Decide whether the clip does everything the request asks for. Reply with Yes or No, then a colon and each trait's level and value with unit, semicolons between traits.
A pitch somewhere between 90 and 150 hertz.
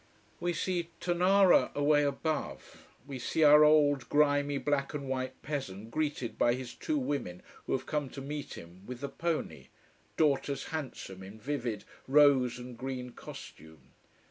Yes: medium, 140 Hz